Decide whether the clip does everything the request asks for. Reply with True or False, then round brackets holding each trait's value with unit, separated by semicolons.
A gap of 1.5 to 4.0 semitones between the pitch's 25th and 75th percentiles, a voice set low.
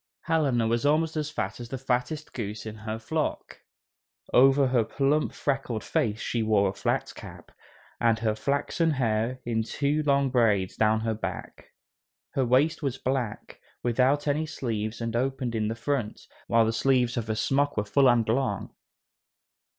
True (3.7 semitones; 120 Hz)